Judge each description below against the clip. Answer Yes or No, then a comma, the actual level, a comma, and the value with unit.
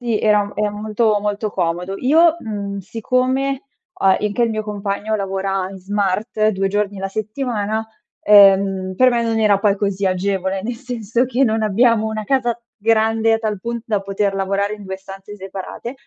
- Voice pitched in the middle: No, high, 210 Hz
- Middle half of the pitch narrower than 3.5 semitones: Yes, narrow, 2.5 semitones